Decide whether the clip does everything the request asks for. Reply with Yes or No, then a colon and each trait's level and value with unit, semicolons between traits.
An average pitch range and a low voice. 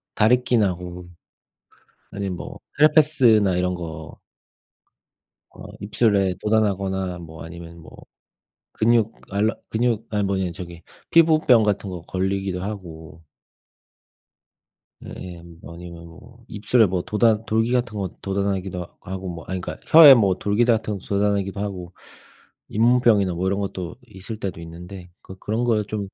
Yes: average, 3.5 semitones; low, 100 Hz